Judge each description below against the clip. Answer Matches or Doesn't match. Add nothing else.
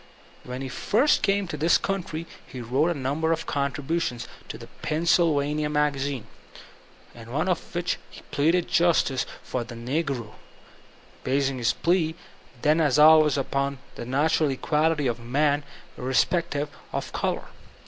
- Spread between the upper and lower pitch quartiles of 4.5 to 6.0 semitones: Doesn't match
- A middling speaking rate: Matches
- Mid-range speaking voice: Matches